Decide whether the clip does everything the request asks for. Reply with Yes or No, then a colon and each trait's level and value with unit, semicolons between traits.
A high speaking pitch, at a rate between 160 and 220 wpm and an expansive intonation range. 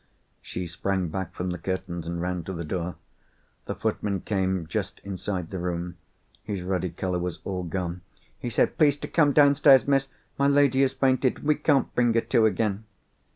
No: very low, 95 Hz; average, 190 wpm; wide, 6.4 semitones